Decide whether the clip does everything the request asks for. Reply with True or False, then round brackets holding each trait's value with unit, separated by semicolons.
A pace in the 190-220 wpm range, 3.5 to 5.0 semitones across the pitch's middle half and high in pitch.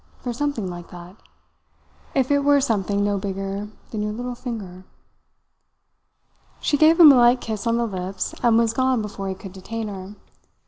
False (175 wpm; 4.1 semitones; 220 Hz)